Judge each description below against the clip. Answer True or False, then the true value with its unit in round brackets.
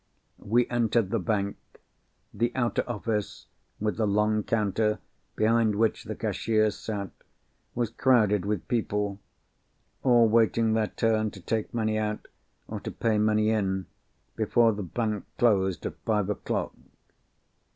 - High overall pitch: False (110 Hz)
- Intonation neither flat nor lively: False (1.7 semitones)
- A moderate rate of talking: False (130 wpm)